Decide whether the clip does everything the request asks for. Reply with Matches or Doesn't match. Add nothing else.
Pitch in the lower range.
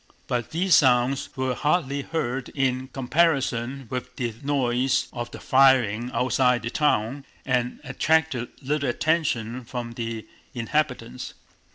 Matches